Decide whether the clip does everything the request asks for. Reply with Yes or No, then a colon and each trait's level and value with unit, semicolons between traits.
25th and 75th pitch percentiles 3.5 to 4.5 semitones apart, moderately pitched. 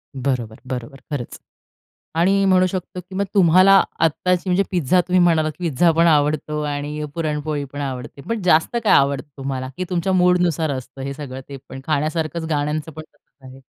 Yes: average, 4.2 semitones; medium, 155 Hz